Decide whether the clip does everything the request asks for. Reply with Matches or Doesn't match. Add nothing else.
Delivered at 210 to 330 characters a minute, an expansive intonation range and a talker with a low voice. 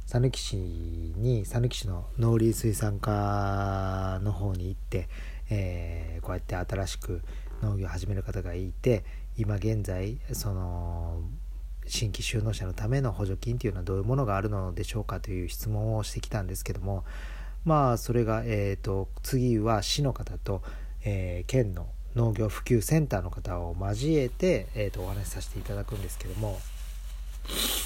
Doesn't match